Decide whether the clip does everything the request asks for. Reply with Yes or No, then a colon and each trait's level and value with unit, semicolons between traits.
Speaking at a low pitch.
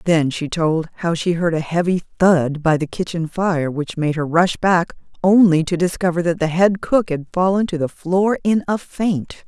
No: medium, 175 Hz